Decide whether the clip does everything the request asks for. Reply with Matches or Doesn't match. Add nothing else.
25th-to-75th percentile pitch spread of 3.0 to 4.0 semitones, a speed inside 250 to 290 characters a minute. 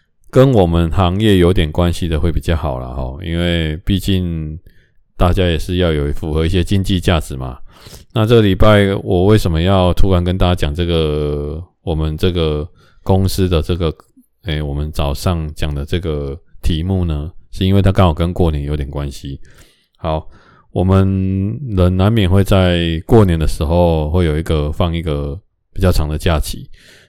Matches